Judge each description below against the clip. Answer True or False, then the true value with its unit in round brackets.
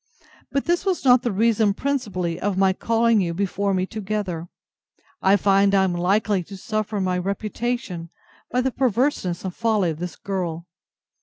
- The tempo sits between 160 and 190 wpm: True (170 wpm)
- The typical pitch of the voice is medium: False (200 Hz)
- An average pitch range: True (3.8 semitones)